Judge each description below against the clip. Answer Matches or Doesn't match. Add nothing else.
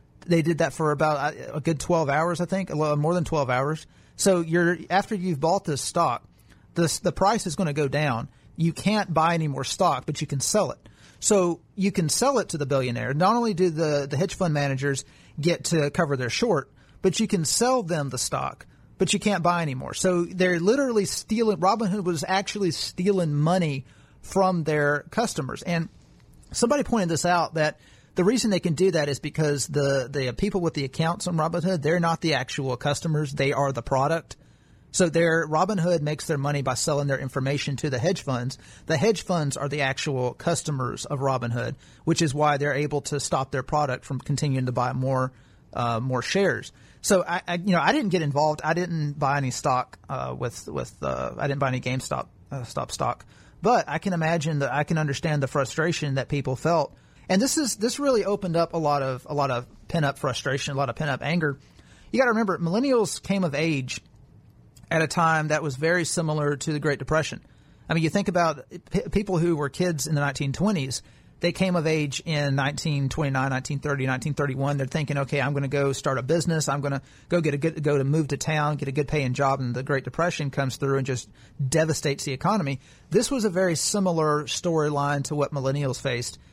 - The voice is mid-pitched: Matches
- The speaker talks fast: Matches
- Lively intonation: Doesn't match